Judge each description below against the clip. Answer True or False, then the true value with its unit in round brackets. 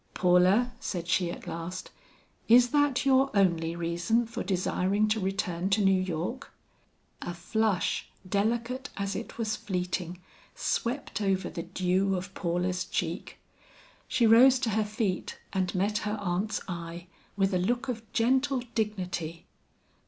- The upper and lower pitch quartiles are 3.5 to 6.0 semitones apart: True (4.1 semitones)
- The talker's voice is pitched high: True (195 Hz)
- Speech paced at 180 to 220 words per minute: False (140 wpm)